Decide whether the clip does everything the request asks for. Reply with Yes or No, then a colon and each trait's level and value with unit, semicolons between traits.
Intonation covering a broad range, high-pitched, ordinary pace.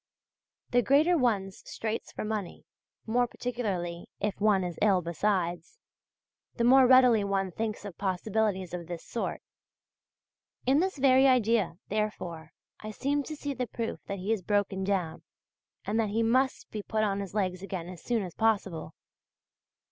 No: average, 4.2 semitones; high, 210 Hz; average, 160 wpm